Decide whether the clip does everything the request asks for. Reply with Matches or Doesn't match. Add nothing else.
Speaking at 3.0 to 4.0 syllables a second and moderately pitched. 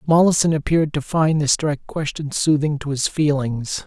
Doesn't match